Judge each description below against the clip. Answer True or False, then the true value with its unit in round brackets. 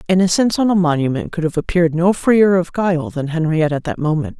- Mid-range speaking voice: True (170 Hz)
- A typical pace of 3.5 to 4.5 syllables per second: False (6.4 syllables/s)